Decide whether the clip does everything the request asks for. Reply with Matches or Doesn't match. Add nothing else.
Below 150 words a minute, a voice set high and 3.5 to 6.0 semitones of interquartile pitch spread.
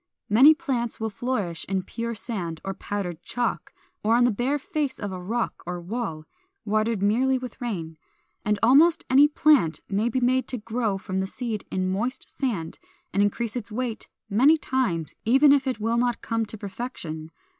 Doesn't match